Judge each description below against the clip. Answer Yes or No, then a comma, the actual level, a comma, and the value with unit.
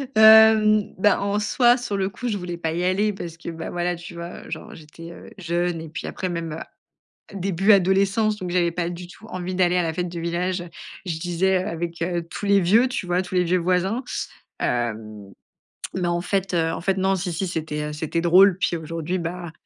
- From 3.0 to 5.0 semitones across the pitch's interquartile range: No, narrow, 2.4 semitones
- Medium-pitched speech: Yes, medium, 180 Hz